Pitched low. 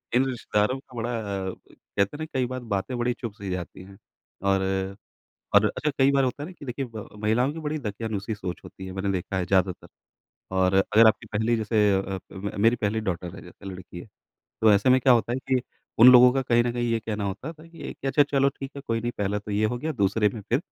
Yes: low, 110 Hz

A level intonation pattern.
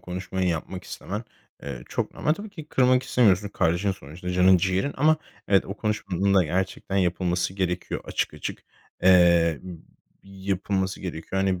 Yes: narrow, 1.9 semitones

